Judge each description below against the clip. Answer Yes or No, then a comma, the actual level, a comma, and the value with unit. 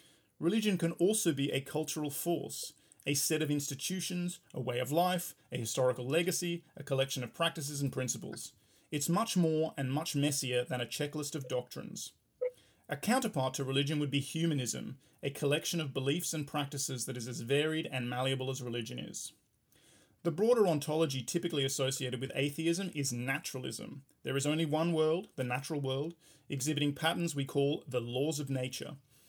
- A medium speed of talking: Yes, average, 170 wpm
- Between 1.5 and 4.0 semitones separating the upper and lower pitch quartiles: Yes, average, 3.6 semitones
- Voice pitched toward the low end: No, medium, 145 Hz